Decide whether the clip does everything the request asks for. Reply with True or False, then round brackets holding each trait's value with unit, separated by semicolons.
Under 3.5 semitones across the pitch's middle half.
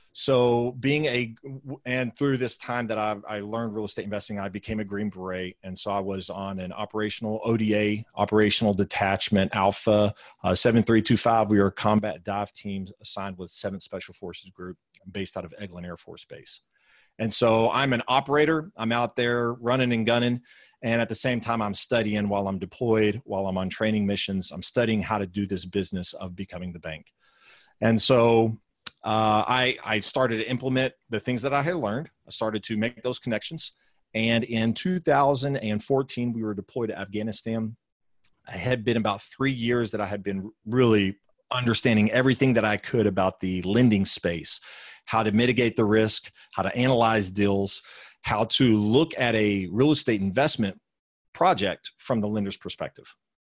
True (3.1 semitones)